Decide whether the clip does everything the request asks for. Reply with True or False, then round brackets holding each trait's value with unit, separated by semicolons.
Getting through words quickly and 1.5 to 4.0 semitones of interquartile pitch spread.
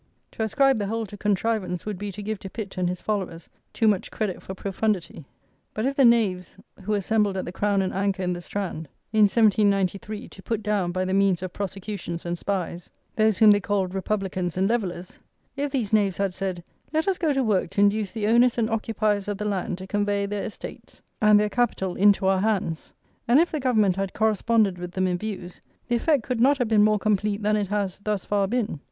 True (220 wpm; 2.5 semitones)